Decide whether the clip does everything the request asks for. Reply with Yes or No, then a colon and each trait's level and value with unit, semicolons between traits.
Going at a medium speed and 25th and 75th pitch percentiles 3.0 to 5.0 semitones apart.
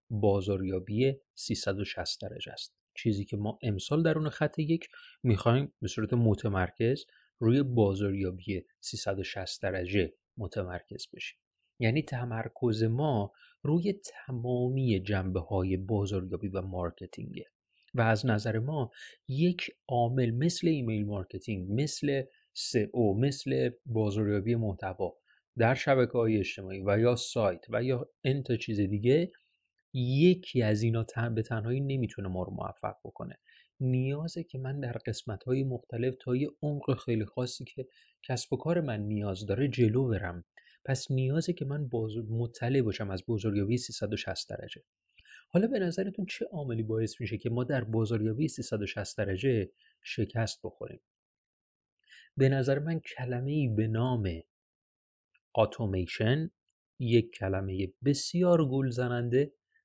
Yes: average, 130 wpm; average, 4.5 semitones